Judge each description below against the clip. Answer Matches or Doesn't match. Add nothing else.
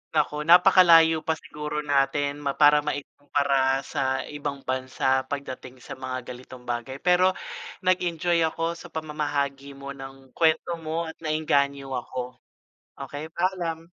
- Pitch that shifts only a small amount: Doesn't match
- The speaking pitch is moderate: Matches